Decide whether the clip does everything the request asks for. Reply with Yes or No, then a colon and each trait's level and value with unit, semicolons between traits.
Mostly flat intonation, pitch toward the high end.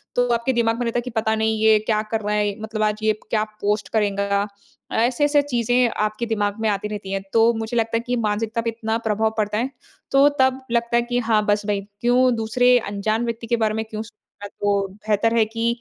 Yes: narrow, 1.9 semitones; high, 220 Hz